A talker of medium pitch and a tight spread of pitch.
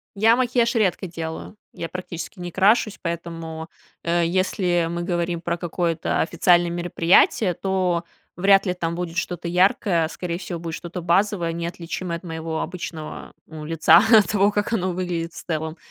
Yes: medium, 175 Hz; narrow, 2.0 semitones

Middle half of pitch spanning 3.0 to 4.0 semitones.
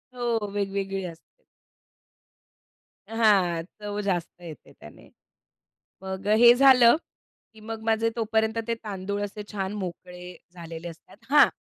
Yes: average, 3.7 semitones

